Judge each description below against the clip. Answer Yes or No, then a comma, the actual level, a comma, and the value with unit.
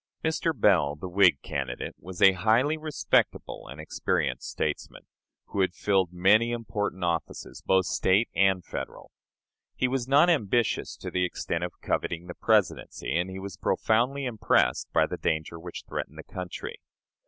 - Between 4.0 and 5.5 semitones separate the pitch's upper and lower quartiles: Yes, average, 4.9 semitones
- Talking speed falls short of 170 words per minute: Yes, average, 155 wpm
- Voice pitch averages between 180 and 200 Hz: No, very low, 95 Hz